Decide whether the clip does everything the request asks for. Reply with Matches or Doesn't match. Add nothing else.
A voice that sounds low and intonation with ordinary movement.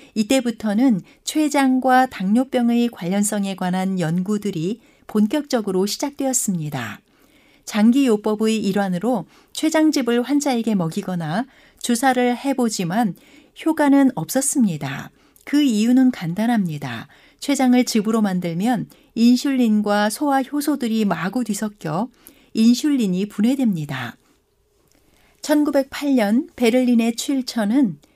Doesn't match